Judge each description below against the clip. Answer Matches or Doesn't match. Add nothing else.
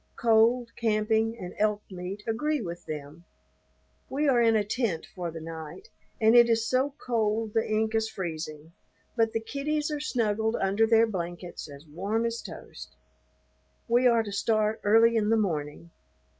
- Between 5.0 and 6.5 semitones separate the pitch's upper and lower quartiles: Doesn't match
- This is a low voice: Doesn't match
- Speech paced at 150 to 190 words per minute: Matches